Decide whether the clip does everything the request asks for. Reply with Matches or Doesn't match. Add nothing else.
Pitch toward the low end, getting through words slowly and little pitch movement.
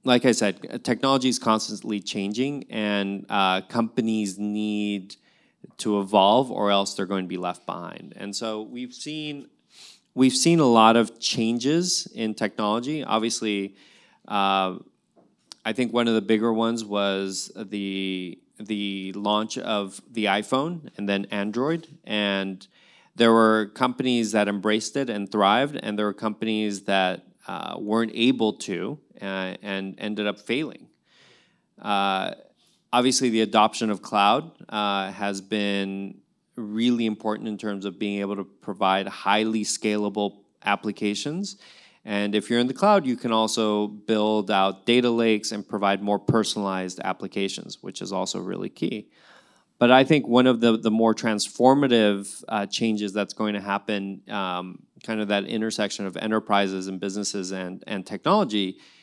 Matches